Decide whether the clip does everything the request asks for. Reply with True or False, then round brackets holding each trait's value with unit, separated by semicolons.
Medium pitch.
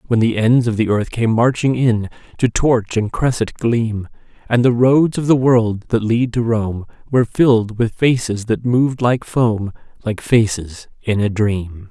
False (115 Hz)